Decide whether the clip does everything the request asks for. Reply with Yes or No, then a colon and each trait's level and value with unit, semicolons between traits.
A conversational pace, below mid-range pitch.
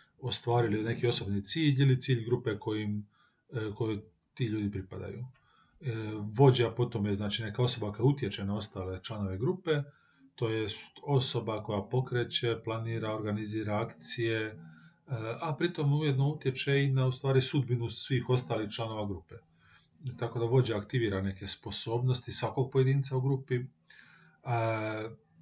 Yes: average, 125 wpm; low, 115 Hz